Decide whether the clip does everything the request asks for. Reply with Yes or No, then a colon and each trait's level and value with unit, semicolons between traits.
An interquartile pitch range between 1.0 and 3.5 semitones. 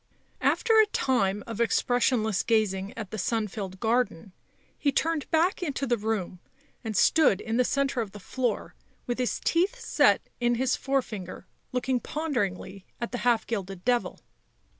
No: average, 4.4 semitones